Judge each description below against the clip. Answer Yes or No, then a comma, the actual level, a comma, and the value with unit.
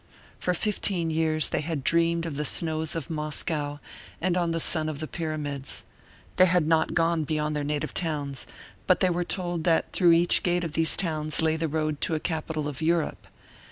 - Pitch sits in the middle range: Yes, medium, 160 Hz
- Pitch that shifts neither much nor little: No, narrow, 1.7 semitones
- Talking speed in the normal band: Yes, average, 195 wpm